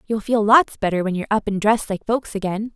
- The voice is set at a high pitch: Yes, high, 210 Hz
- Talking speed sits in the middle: No, fast, 260 wpm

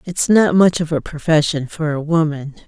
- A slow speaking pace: No, average, 200 wpm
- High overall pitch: No, medium, 160 Hz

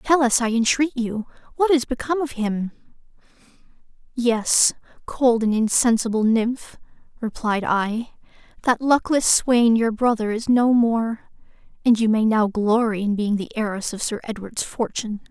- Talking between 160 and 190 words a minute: No, average, 150 wpm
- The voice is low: No, high, 230 Hz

